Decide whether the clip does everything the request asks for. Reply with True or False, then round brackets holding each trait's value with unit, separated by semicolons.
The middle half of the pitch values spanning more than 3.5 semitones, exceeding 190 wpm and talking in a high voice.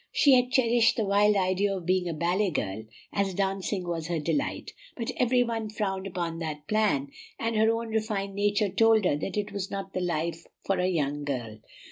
True (4.2 semitones; 200 wpm; 195 Hz)